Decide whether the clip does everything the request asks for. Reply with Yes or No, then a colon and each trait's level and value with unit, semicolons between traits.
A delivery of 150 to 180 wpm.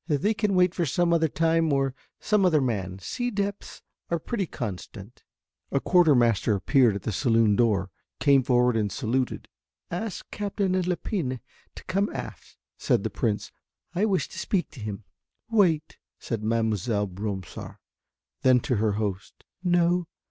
Yes: average, 155 wpm